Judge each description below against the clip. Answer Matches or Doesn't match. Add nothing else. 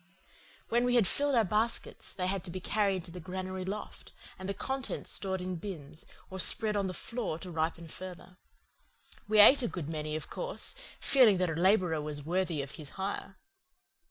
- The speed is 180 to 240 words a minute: Matches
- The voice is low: Doesn't match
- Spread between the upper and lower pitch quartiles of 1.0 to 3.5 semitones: Doesn't match